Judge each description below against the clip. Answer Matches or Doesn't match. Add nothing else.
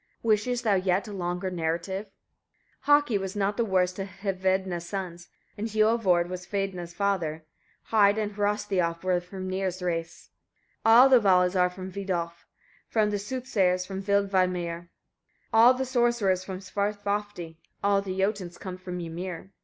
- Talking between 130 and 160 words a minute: Matches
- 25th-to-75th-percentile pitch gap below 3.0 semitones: Matches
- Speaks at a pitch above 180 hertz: Matches